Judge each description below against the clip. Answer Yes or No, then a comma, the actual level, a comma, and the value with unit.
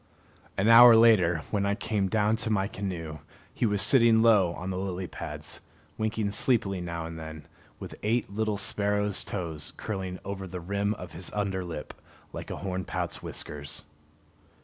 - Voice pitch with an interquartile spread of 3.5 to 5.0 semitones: No, average, 3.0 semitones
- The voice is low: Yes, low, 100 Hz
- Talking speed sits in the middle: Yes, average, 165 wpm